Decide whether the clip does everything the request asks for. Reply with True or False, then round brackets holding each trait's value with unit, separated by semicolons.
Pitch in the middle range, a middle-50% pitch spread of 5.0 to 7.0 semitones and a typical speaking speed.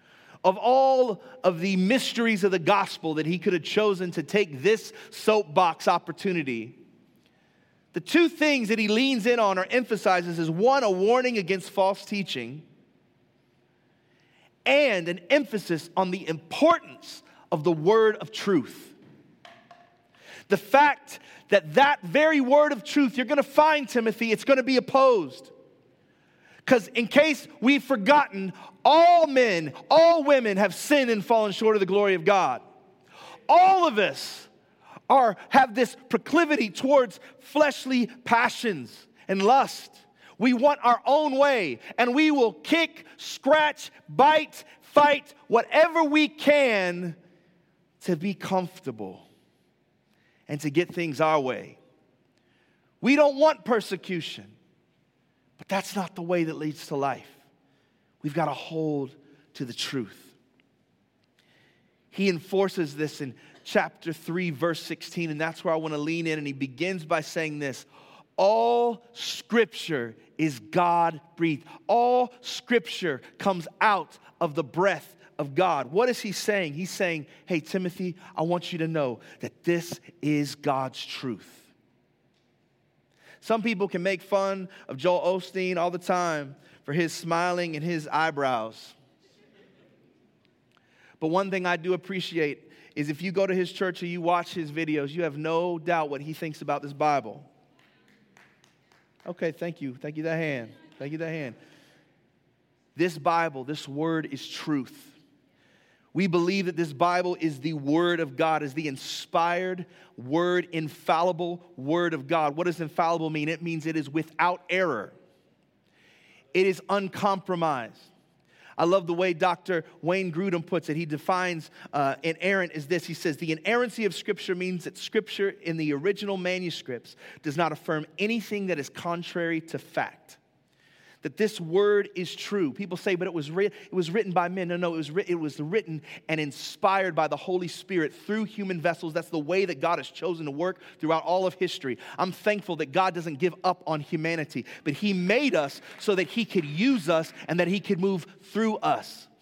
False (180 Hz; 4.6 semitones; 160 wpm)